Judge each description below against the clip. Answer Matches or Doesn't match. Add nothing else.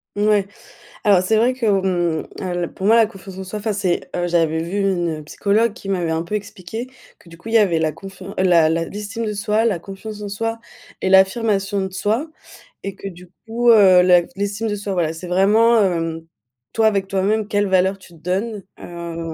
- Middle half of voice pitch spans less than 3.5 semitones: Matches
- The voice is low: Doesn't match